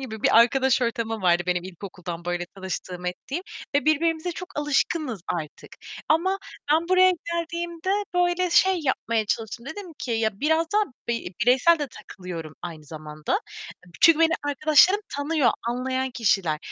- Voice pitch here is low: No, very high, 260 Hz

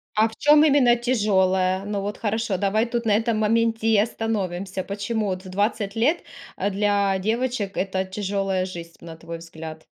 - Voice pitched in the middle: No, high, 205 Hz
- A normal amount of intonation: Yes, average, 3.0 semitones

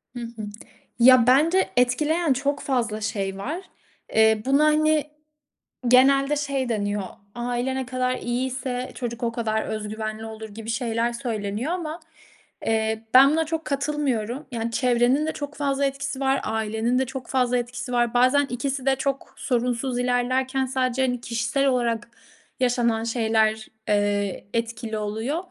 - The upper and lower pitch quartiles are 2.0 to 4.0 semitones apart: Yes, average, 3.3 semitones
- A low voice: No, high, 245 Hz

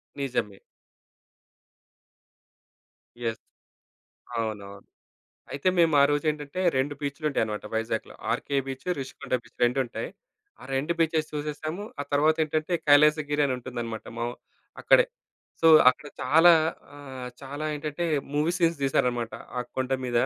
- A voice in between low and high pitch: Yes, medium, 145 Hz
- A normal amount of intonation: Yes, average, 3.5 semitones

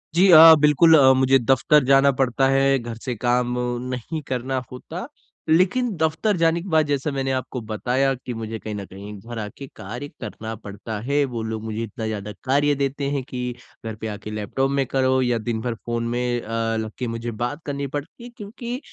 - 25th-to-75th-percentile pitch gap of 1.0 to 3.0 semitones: No, average, 3.9 semitones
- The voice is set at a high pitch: No, low, 130 Hz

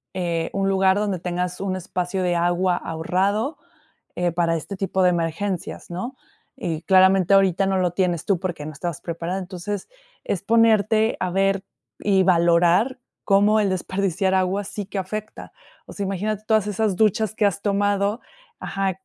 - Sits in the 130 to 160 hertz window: No, high, 190 Hz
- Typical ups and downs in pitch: No, narrow, 2.3 semitones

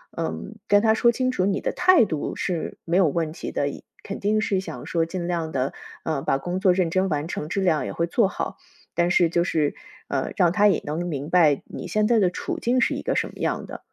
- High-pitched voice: No, medium, 175 Hz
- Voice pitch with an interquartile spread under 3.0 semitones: No, average, 3.9 semitones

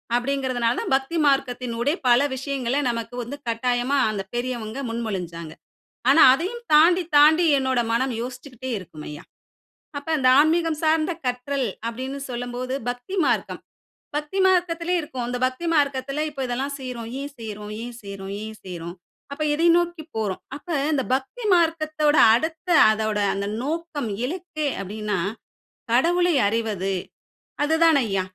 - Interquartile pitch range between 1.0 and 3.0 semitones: No, average, 4.9 semitones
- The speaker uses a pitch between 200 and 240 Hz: No, very high, 260 Hz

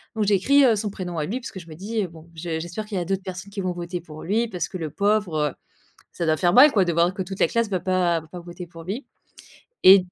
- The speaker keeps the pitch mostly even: No, average, 3.1 semitones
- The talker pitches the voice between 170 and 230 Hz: Yes, medium, 185 Hz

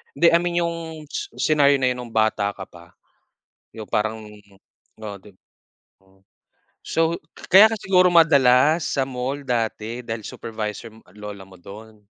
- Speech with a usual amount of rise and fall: No, wide, 6.7 semitones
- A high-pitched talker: No, low, 120 Hz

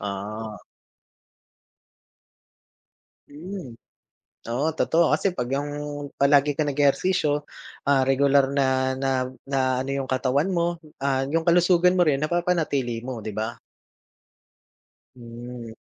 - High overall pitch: No, medium, 140 Hz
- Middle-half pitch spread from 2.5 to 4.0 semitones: No, average, 4.5 semitones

